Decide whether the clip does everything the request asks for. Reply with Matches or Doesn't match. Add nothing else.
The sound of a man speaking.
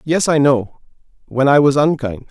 Matches